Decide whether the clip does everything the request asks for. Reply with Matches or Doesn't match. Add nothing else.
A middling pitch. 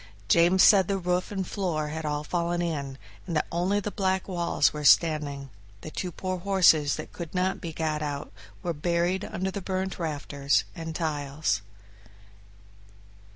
Matches